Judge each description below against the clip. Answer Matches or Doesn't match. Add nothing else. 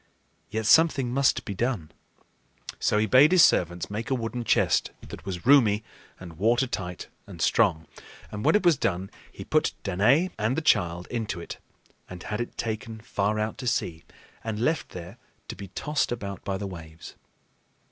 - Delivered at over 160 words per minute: Matches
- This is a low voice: Matches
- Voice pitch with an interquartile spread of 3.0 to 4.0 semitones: Doesn't match